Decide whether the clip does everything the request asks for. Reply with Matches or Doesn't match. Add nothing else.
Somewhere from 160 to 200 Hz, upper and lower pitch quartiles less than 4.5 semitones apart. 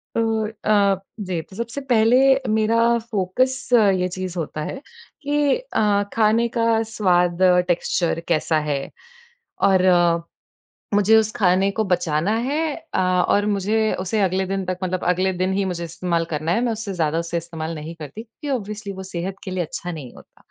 Matches